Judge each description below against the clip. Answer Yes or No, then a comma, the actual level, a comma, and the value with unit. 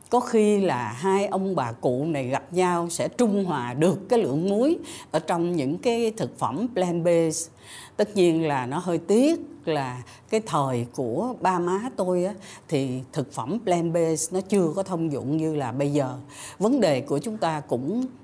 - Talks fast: No, average, 195 wpm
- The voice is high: No, medium, 175 Hz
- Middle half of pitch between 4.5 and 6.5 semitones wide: Yes, wide, 5.4 semitones